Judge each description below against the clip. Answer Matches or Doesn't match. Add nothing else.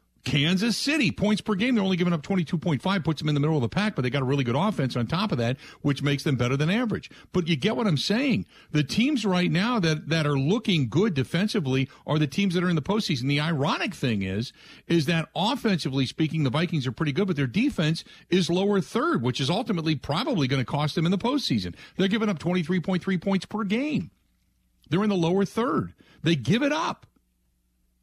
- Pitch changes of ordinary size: Doesn't match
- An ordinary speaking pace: Doesn't match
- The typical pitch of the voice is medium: Matches